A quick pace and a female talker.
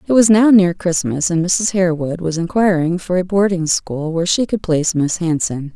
Yes: fast, 210 wpm; female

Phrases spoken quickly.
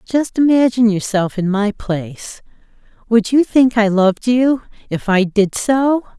No: average, 155 wpm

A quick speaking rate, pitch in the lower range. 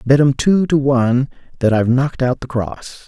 Yes: fast, 215 wpm; low, 130 Hz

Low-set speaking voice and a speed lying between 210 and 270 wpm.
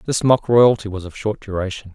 Yes: low, 105 Hz; fast, 215 wpm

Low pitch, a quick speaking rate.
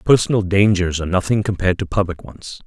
No: very low, 95 Hz; average, 180 wpm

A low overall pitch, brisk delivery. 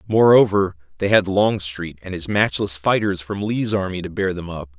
No: very low, 95 Hz; average, 190 wpm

